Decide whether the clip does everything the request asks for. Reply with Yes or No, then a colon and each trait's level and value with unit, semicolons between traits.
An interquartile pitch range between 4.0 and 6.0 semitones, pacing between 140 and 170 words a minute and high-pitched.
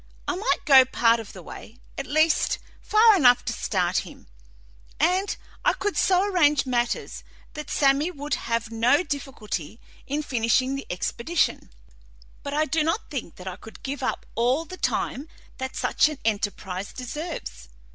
Yes: average, 5.1 semitones; average, 160 wpm; very high, 275 Hz